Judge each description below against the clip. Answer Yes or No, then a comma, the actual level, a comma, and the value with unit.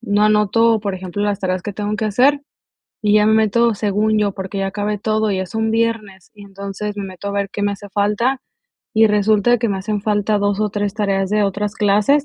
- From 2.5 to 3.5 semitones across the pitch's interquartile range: No, narrow, 1.4 semitones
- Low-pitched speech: No, high, 210 Hz